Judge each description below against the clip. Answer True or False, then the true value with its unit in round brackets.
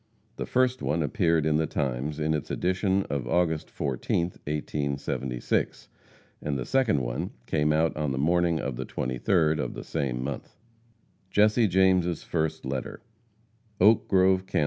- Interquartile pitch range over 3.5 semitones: True (4.6 semitones)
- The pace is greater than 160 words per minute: False (150 wpm)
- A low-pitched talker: True (80 Hz)